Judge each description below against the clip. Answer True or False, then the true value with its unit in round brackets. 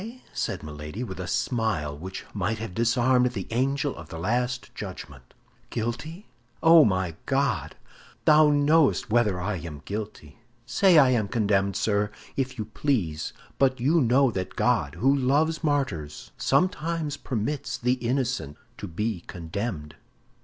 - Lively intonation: True (6.5 semitones)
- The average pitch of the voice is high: False (120 Hz)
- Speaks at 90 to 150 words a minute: True (140 wpm)